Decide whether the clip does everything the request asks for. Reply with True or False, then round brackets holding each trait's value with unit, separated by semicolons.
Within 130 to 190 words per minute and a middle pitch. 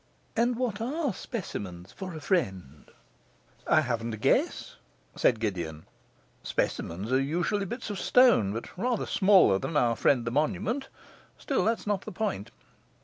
True (150 wpm; 155 Hz)